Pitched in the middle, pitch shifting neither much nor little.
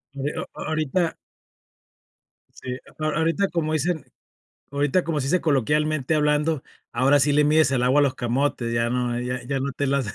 Yes: medium, 145 Hz; average, 3.0 semitones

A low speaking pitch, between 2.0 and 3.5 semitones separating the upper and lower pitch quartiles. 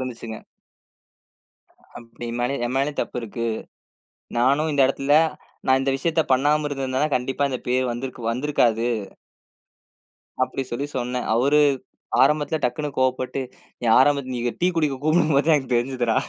Yes: low, 130 Hz; average, 2.8 semitones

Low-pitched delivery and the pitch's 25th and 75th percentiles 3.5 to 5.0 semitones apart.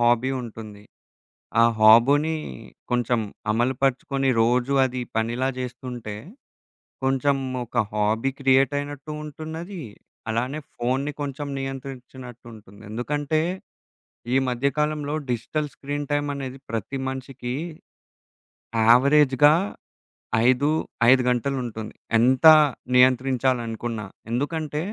No: low, 130 Hz; average, 3.0 semitones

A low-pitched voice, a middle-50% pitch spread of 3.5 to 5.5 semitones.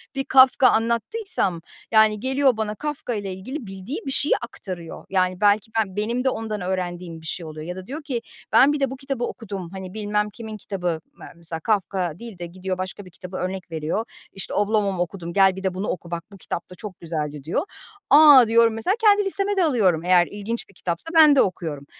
No: high, 200 Hz; average, 4.8 semitones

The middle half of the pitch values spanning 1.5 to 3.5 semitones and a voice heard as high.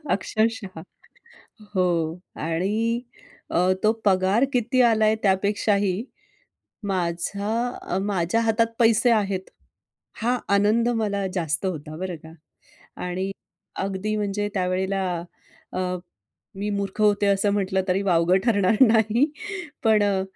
Yes: average, 2.7 semitones; high, 200 Hz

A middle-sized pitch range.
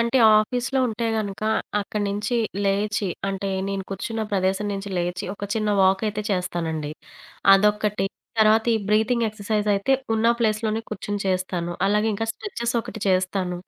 No: narrow, 2.3 semitones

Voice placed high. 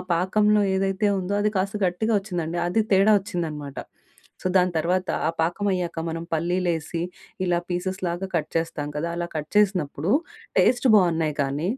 No: medium, 180 Hz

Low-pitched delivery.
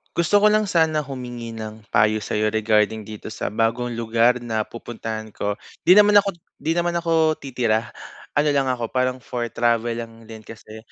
Yes: low, 120 Hz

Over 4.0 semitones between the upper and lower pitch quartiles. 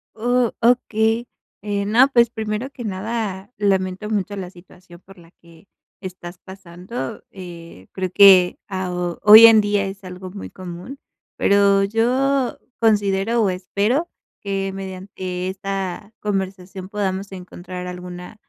No: average, 2.7 semitones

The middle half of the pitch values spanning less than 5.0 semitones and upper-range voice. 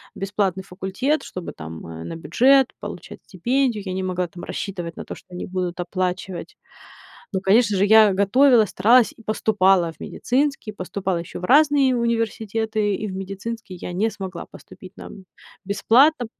Yes: average, 3.9 semitones; high, 200 Hz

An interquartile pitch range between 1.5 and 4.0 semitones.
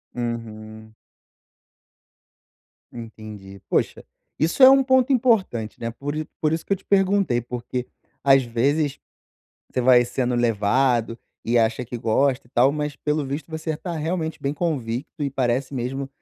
No: average, 4.8 semitones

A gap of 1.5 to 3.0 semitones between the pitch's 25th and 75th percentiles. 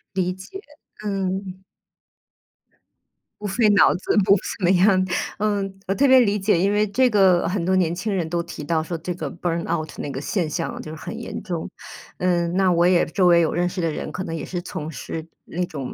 Yes: narrow, 2.6 semitones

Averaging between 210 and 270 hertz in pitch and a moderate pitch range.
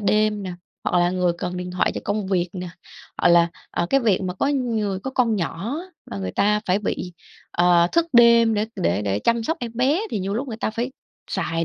No: high, 200 Hz; average, 4.5 semitones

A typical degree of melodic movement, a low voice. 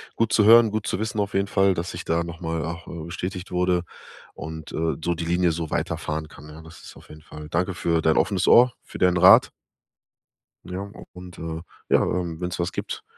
No: narrow, 2.3 semitones; very low, 85 Hz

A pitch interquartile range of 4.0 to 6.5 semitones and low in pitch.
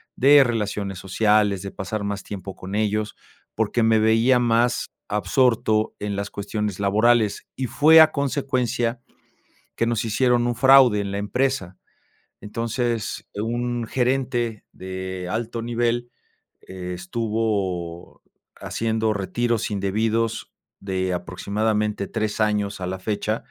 No: average, 3.0 semitones; low, 110 Hz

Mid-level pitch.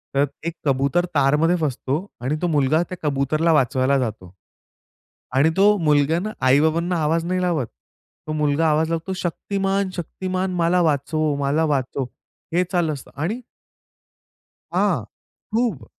Yes: medium, 155 Hz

